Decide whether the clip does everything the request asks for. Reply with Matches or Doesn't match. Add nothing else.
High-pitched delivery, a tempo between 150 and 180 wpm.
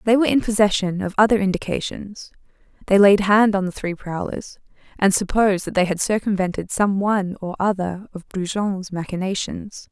Matches